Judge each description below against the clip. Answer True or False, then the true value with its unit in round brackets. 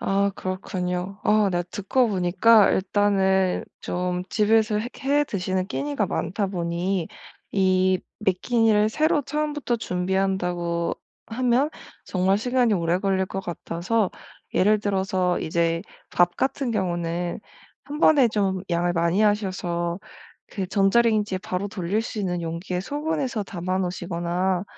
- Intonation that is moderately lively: True (3.3 semitones)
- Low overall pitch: False (190 Hz)